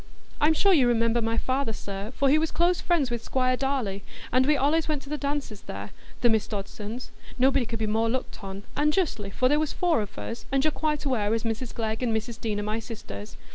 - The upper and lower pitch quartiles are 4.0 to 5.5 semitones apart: Yes, average, 4.6 semitones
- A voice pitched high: Yes, high, 240 Hz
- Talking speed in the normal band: No, fast, 225 wpm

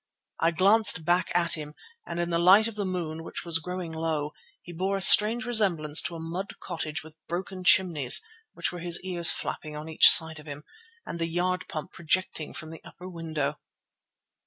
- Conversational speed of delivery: Yes, average, 195 wpm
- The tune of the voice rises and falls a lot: No, narrow, 2.5 semitones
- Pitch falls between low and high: Yes, medium, 170 Hz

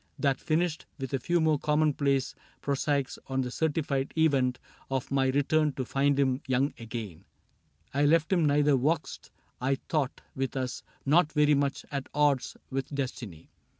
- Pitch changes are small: Yes, narrow, 2.1 semitones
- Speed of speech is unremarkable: Yes, average, 165 wpm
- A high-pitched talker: No, medium, 140 Hz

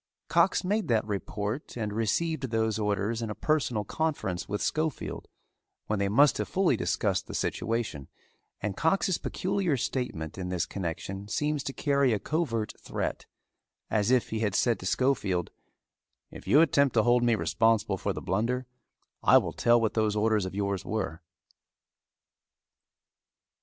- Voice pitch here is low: Yes, low, 110 Hz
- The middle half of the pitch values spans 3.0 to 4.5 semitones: No, average, 5.1 semitones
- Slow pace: No, average, 155 wpm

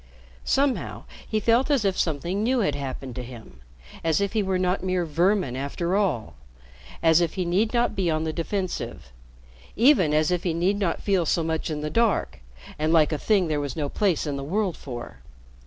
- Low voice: No, medium, 170 Hz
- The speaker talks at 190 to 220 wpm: Yes, fast, 205 wpm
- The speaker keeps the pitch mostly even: No, average, 4.8 semitones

